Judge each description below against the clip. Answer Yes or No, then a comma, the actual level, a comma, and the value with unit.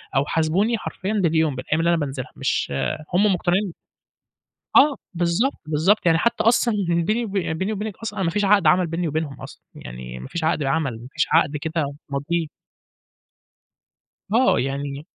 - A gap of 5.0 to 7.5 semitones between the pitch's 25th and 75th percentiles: Yes, wide, 5.4 semitones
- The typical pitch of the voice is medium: Yes, medium, 165 Hz